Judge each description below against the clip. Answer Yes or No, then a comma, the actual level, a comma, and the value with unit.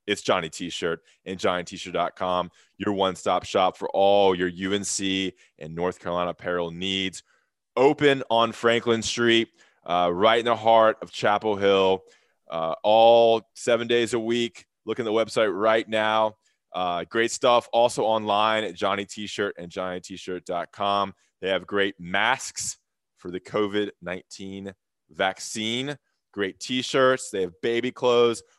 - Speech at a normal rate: Yes, average, 155 wpm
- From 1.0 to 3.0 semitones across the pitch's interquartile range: No, average, 3.5 semitones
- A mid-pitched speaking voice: No, low, 105 Hz